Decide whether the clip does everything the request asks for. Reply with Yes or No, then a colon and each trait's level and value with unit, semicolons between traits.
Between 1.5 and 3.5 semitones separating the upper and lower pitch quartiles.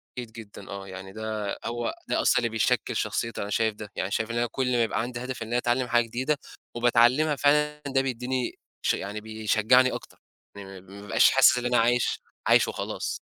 Yes: average, 2.8 semitones